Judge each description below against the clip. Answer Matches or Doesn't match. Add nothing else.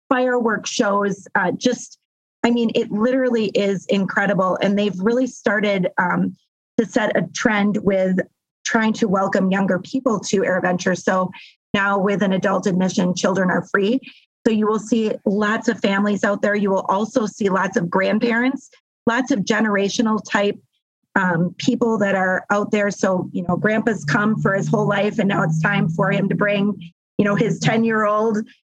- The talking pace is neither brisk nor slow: Matches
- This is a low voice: Doesn't match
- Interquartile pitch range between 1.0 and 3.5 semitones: Matches